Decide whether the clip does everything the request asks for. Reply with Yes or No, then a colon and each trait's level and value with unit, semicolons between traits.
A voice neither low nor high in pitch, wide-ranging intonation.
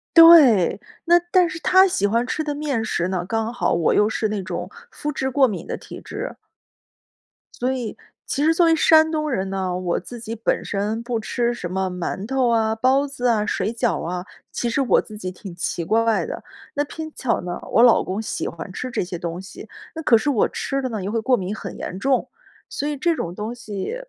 No: high, 230 Hz; wide, 6.0 semitones